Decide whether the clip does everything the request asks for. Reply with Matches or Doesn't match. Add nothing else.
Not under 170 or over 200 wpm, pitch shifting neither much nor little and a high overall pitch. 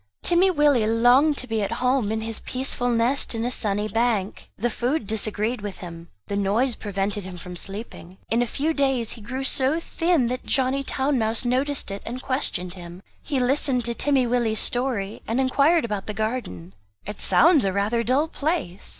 Matches